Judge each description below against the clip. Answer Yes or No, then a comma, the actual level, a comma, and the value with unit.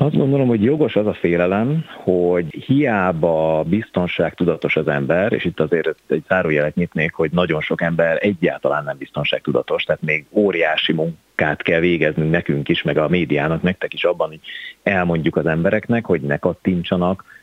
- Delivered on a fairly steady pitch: No, average, 4.2 semitones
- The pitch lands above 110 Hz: No, very low, 90 Hz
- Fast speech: Yes, fast, 160 wpm